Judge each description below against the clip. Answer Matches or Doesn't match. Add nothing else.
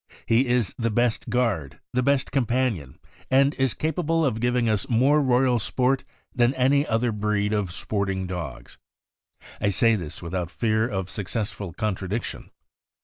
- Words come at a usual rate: Matches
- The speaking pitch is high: Doesn't match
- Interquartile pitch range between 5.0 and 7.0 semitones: Doesn't match